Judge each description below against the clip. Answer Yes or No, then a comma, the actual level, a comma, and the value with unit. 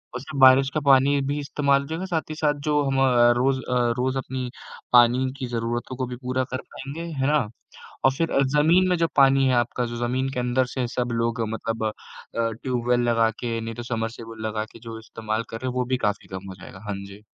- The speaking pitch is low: Yes, low, 125 Hz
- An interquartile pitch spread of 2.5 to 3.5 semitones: Yes, average, 2.8 semitones